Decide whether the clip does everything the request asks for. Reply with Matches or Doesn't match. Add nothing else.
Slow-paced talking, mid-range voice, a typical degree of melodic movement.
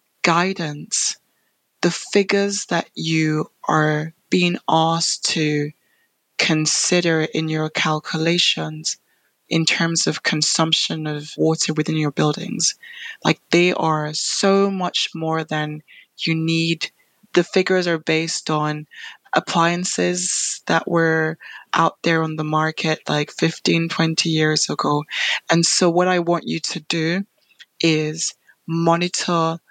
Doesn't match